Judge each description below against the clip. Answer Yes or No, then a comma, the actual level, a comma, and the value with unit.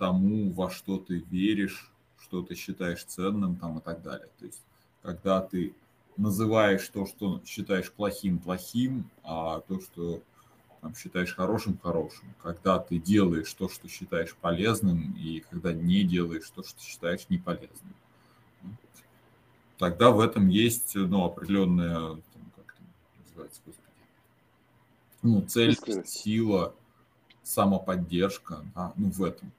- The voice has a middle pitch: No, very low, 95 Hz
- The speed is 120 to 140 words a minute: Yes, average, 130 wpm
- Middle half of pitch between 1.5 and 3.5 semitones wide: Yes, average, 3.1 semitones